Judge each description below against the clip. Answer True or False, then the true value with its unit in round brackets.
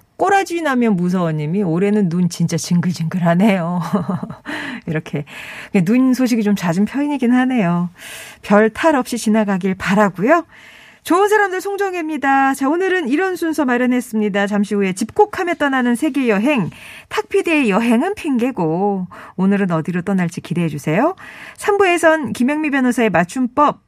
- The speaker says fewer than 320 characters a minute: False (325 characters per minute)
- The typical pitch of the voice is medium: False (230 Hz)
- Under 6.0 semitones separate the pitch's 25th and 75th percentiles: False (7.4 semitones)